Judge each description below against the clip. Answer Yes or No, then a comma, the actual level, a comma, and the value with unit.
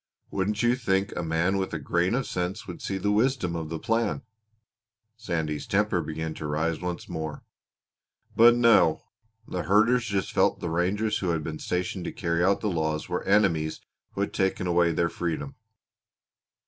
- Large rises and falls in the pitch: No, average, 4.0 semitones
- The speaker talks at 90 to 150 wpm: No, average, 175 wpm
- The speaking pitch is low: Yes, very low, 90 Hz